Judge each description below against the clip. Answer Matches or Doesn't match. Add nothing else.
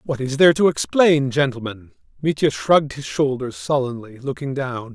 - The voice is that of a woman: Doesn't match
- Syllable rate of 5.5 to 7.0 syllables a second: Doesn't match